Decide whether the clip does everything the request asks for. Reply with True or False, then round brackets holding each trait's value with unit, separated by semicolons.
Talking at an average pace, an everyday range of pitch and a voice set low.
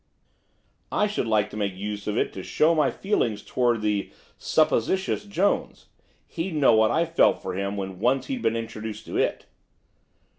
False (180 wpm; 7.8 semitones; 115 Hz)